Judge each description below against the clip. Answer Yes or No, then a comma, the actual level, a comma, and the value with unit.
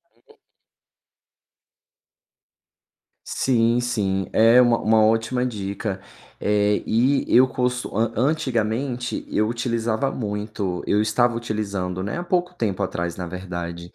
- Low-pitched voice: Yes, low, 110 Hz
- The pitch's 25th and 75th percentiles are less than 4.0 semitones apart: Yes, average, 3.5 semitones